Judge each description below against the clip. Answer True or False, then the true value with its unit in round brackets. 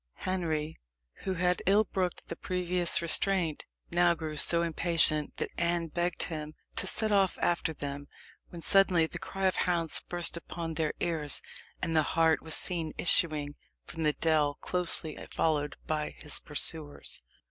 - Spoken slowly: False (155 wpm)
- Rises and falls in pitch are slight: True (2.3 semitones)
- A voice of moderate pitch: True (165 Hz)